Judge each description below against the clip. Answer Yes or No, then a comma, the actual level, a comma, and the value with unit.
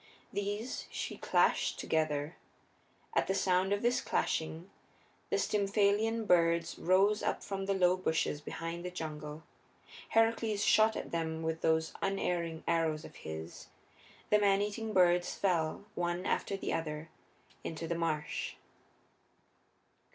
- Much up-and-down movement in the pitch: No, average, 3.8 semitones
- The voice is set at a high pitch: No, medium, 175 Hz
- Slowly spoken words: Yes, slow, 130 wpm